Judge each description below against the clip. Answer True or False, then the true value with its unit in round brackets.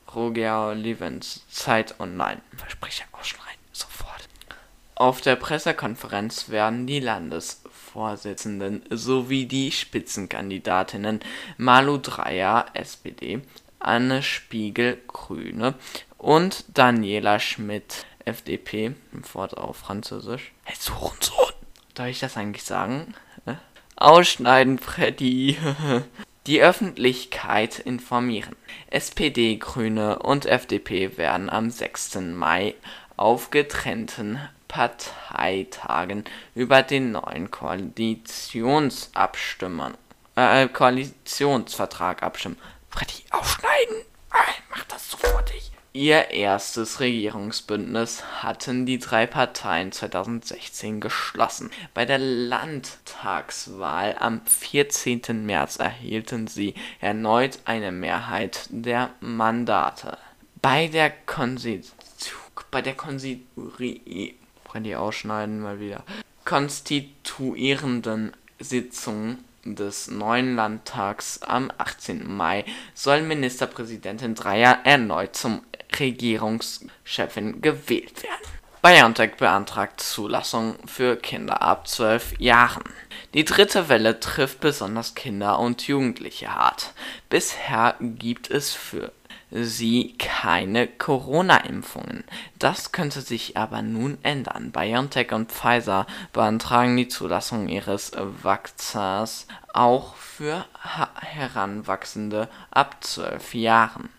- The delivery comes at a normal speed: False (90 wpm)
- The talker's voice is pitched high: False (120 Hz)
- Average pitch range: True (3.4 semitones)